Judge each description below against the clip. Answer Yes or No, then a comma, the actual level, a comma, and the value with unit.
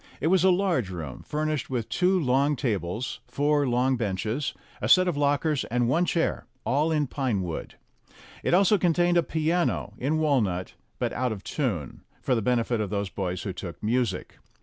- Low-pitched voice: Yes, low, 130 Hz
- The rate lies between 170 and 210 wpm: Yes, average, 180 wpm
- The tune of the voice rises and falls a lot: Yes, wide, 6.7 semitones